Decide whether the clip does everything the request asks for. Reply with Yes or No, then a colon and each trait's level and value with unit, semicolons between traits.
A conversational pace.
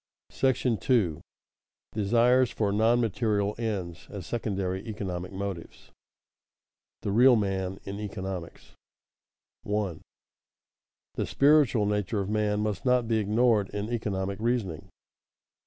No: slow, 115 wpm